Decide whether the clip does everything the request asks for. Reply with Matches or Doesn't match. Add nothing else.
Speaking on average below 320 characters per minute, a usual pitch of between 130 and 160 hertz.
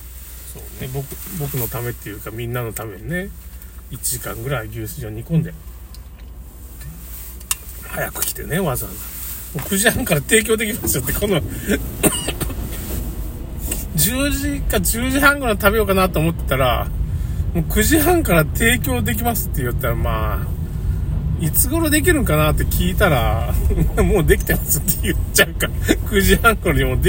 Doesn't match